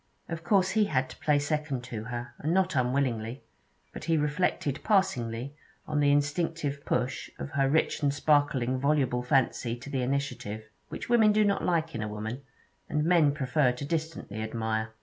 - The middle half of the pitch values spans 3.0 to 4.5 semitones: Yes, average, 4.2 semitones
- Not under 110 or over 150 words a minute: No, average, 175 wpm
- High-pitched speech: No, medium, 140 Hz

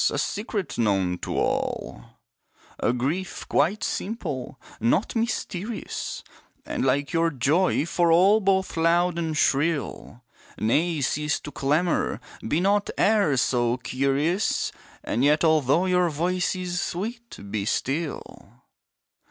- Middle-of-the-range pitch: Yes, medium, 165 Hz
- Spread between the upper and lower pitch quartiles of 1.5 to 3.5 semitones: No, average, 5.1 semitones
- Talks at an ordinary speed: No, slow, 120 wpm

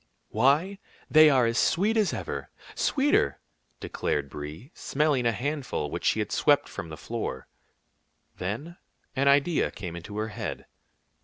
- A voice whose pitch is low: Yes, low, 130 Hz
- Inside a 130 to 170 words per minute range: Yes, average, 145 wpm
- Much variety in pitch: Yes, wide, 9.0 semitones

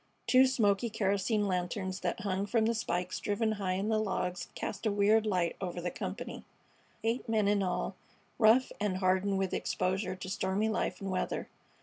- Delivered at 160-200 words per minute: Yes, average, 175 wpm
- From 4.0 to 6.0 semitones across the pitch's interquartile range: No, average, 2.7 semitones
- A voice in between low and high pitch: No, high, 200 Hz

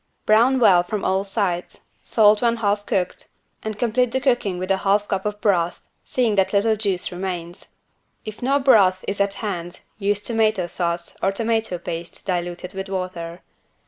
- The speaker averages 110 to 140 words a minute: No, average, 170 wpm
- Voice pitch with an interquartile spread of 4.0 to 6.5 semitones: No, average, 3.2 semitones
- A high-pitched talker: Yes, high, 200 Hz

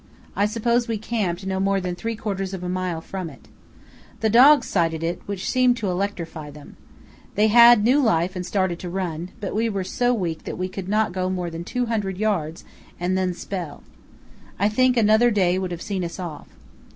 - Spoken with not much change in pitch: No, average, 3.6 semitones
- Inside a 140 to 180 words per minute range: No, average, 200 wpm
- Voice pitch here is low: No, high, 190 Hz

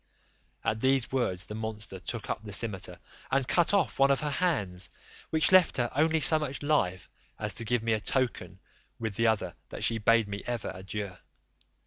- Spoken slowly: No, average, 195 wpm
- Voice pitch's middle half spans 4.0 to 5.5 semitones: Yes, average, 5.1 semitones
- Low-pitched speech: Yes, low, 115 Hz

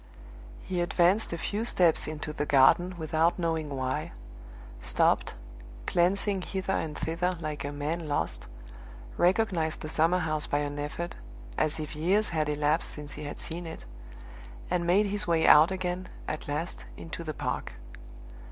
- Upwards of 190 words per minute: No, average, 155 wpm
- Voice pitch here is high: No, medium, 165 Hz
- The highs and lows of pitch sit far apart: No, average, 3.0 semitones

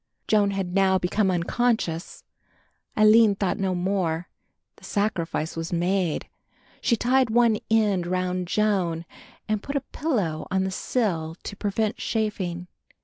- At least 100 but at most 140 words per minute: Yes, slow, 135 wpm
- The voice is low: No, high, 195 Hz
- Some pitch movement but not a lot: Yes, average, 3.4 semitones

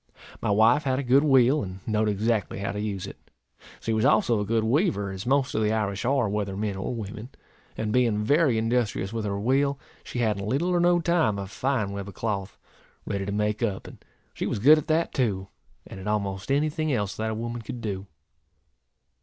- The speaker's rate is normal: No, fast, 220 wpm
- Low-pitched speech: Yes, low, 110 Hz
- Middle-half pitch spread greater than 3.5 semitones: Yes, average, 4.5 semitones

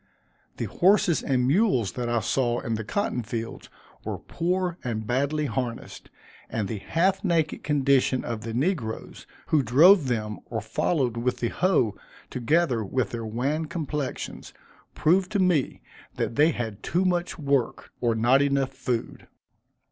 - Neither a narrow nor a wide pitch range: No, wide, 6.0 semitones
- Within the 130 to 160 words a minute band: Yes, average, 150 wpm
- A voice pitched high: No, low, 130 Hz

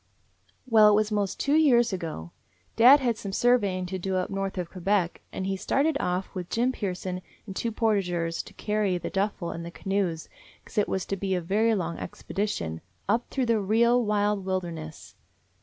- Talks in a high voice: Yes, high, 195 Hz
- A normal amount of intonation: Yes, average, 3.5 semitones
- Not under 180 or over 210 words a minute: Yes, average, 190 wpm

